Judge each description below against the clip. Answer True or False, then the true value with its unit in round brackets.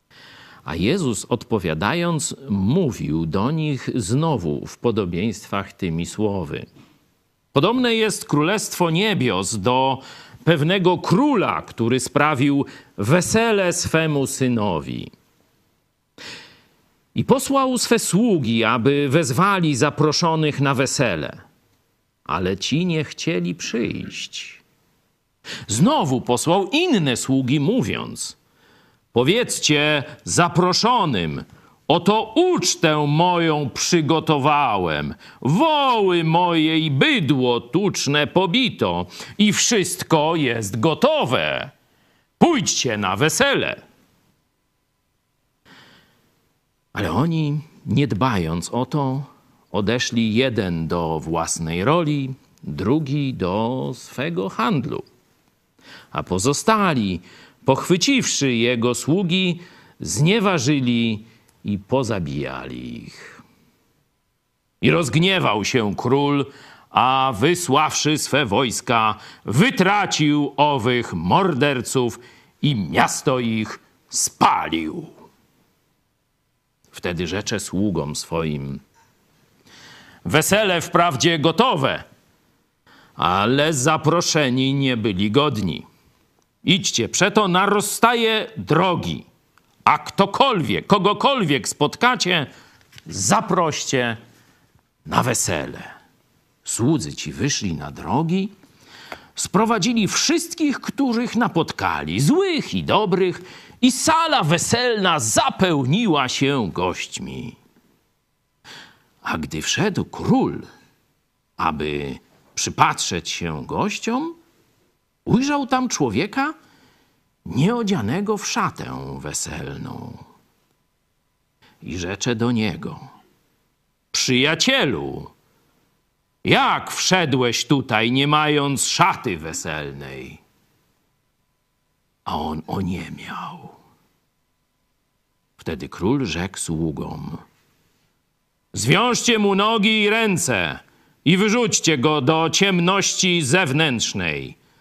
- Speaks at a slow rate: True (80 wpm)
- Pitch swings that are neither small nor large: False (7.5 semitones)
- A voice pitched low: False (150 Hz)